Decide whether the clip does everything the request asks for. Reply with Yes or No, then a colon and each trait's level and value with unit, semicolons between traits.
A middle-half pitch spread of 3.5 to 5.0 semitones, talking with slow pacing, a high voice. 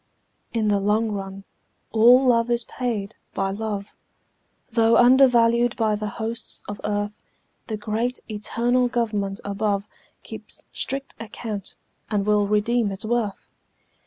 No: narrow, 2.4 semitones; slow, 130 wpm; high, 220 Hz